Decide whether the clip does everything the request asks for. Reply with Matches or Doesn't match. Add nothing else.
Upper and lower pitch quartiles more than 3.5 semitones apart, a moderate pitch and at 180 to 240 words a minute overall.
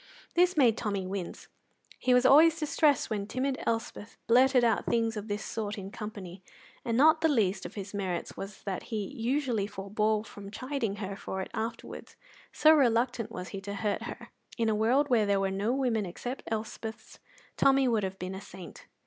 Doesn't match